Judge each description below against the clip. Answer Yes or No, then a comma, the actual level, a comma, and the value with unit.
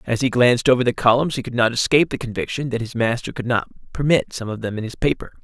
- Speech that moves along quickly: Yes, fast, 265 wpm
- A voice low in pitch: Yes, low, 125 Hz